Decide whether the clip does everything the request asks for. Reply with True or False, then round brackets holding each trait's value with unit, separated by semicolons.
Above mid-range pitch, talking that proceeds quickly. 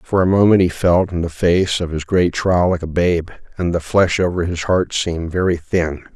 False (85 Hz; 235 wpm)